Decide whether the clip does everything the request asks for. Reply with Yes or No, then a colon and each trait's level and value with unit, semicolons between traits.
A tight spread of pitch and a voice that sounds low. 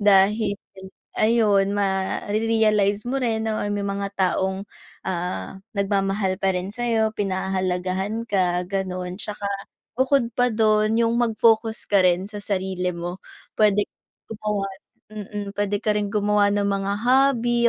No: narrow, 2.3 semitones; high, 205 Hz